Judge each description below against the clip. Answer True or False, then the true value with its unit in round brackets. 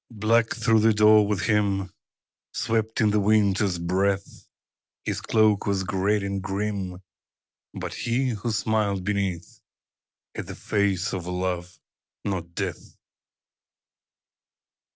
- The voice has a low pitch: True (100 Hz)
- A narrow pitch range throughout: True (2.3 semitones)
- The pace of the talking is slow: True (120 wpm)